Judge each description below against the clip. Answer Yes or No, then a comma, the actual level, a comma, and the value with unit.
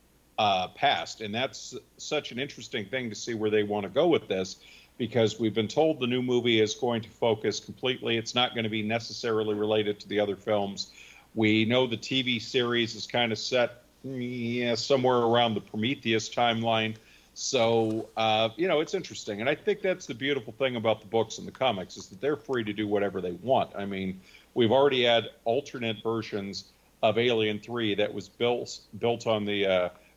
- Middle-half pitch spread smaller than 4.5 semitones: Yes, narrow, 2.4 semitones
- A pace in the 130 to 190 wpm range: No, average, 200 wpm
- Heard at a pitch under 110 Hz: No, low, 115 Hz